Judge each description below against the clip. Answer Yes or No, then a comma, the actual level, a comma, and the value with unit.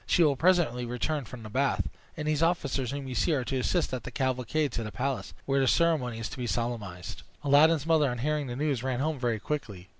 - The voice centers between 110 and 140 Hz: Yes, low, 135 Hz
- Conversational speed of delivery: No, fast, 235 wpm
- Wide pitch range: No, average, 3.8 semitones